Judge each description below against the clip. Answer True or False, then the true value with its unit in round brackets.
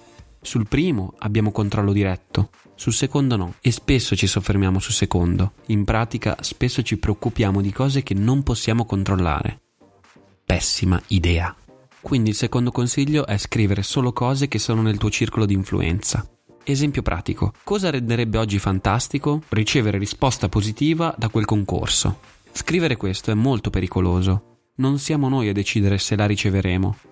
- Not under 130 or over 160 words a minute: True (150 wpm)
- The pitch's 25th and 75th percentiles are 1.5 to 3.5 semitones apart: False (4.2 semitones)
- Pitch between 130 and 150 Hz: False (110 Hz)